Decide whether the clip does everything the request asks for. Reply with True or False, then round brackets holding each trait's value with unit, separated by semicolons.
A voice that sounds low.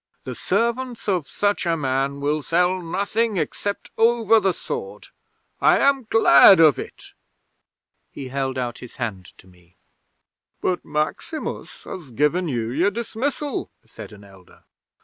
False (170 Hz)